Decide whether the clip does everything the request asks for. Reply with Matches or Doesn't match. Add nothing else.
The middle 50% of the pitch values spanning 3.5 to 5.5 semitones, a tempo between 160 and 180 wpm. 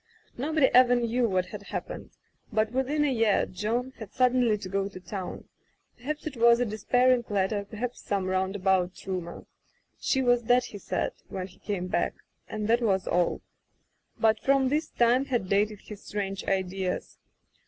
Matches